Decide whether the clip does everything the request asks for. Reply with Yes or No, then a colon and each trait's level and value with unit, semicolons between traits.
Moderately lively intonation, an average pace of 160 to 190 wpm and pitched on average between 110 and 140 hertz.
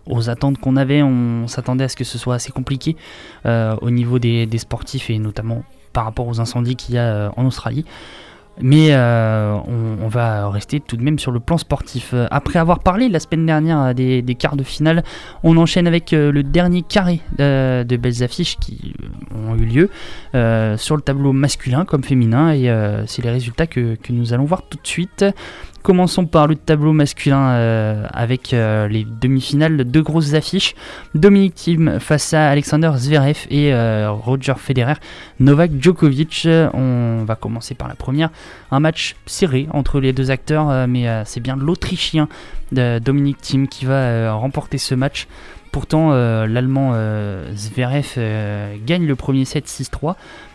Yes: average, 4.4 semitones; average, 180 wpm; low, 135 Hz